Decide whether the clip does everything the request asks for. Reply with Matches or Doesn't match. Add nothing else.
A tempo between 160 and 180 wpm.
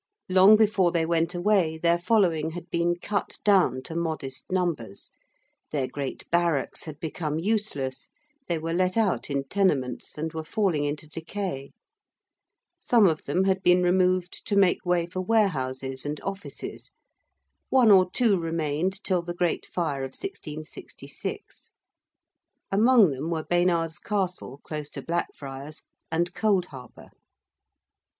Doesn't match